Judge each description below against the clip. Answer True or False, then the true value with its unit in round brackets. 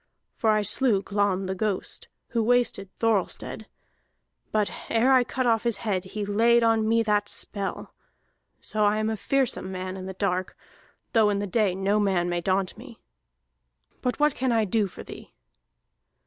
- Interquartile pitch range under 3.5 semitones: True (2.9 semitones)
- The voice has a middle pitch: False (210 Hz)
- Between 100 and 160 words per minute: False (175 wpm)